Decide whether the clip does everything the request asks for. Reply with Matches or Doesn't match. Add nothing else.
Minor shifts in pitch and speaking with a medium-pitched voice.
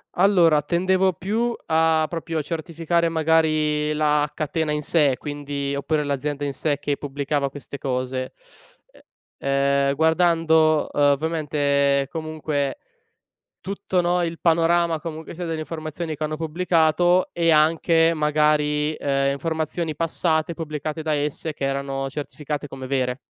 Matches